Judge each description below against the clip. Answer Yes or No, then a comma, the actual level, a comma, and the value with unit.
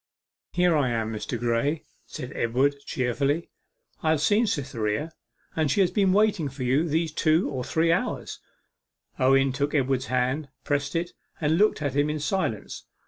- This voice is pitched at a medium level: Yes, medium, 145 Hz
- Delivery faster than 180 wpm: No, average, 165 wpm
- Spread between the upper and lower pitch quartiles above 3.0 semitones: Yes, average, 4.1 semitones